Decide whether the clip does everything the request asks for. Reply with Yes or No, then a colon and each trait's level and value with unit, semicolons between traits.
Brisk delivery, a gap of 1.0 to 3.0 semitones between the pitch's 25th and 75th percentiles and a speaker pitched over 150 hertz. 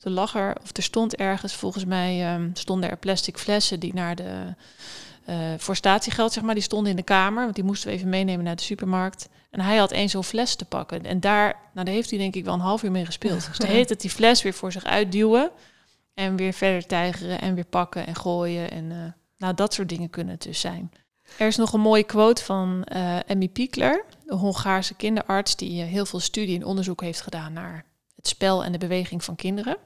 Yes: fast, 230 wpm; average, 2.7 semitones; high, 190 Hz